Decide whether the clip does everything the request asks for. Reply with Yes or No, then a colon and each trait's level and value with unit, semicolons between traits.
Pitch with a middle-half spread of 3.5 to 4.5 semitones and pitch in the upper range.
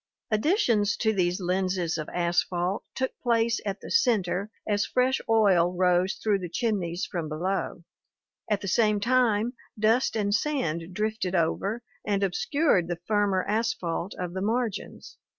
Yes: average, 3.9 semitones; high, 200 Hz